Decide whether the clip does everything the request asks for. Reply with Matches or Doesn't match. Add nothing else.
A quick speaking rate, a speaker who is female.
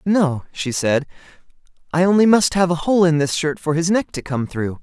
Doesn't match